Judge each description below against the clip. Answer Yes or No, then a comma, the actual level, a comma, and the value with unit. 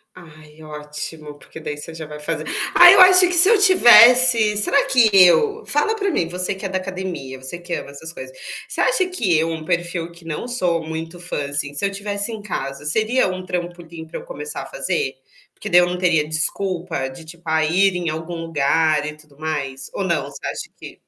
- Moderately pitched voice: Yes, medium, 175 Hz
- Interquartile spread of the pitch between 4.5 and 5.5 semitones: Yes, average, 5.0 semitones